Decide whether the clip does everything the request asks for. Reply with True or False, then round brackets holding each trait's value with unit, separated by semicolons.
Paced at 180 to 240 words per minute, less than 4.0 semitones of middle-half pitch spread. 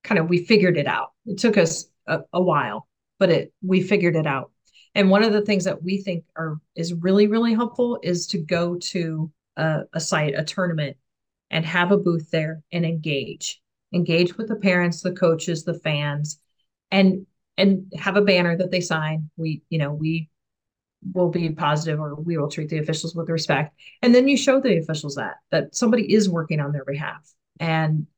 True (200 wpm; 3.5 semitones)